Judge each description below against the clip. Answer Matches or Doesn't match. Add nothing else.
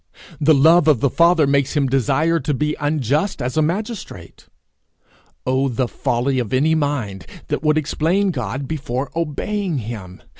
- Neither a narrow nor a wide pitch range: Matches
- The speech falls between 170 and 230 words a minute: Doesn't match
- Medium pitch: Matches